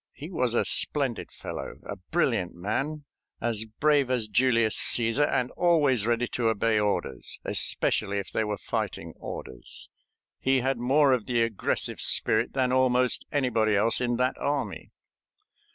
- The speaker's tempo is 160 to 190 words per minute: No, average, 150 wpm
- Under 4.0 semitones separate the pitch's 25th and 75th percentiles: Yes, average, 3.2 semitones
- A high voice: No, low, 120 Hz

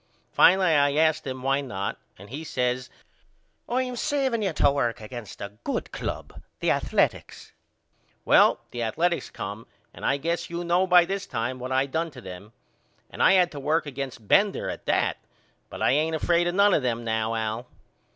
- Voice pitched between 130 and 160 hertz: Yes, medium, 140 Hz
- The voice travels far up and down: Yes, wide, 6.4 semitones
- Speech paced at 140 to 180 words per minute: No, average, 190 wpm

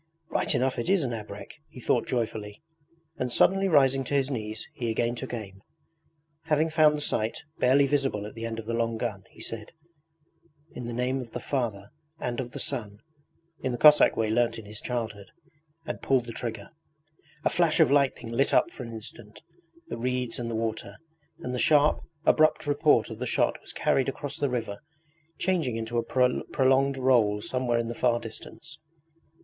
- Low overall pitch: Yes, low, 120 Hz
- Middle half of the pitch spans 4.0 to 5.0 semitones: No, average, 3.3 semitones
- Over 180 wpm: Yes, average, 190 wpm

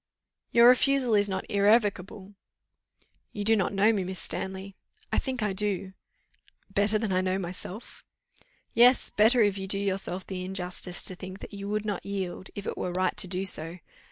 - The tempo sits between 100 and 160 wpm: No, average, 185 wpm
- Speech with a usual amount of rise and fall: No, narrow, 2.0 semitones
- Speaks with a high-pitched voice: Yes, high, 195 Hz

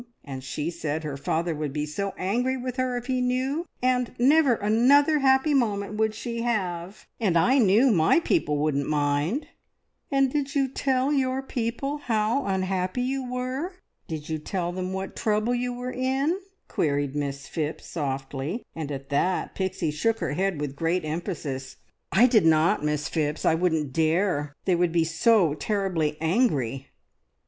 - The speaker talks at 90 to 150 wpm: No, average, 165 wpm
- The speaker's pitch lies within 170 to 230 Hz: Yes, high, 190 Hz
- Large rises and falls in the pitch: Yes, wide, 8.5 semitones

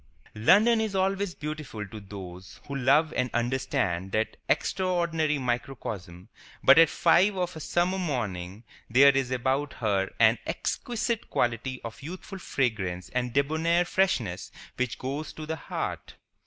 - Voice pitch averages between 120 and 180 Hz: Yes, low, 135 Hz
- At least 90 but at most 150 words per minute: Yes, average, 140 wpm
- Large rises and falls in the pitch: Yes, wide, 7.1 semitones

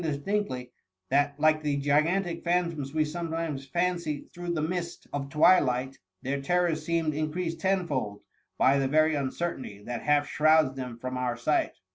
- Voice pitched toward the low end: No, medium, 155 Hz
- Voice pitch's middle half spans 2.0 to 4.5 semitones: Yes, average, 3.8 semitones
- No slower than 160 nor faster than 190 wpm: No, average, 150 wpm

